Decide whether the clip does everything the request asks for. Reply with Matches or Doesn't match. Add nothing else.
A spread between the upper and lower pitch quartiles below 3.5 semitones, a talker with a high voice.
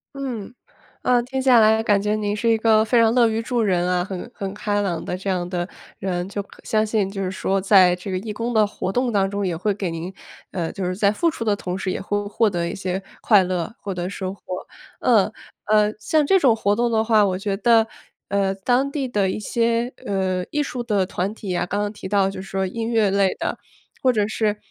Matches